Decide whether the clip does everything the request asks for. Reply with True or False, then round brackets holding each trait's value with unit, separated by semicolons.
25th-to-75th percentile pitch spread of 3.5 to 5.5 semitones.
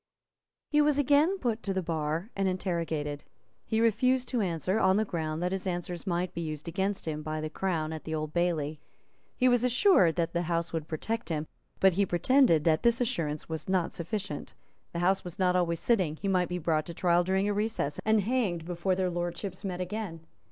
True (4.1 semitones)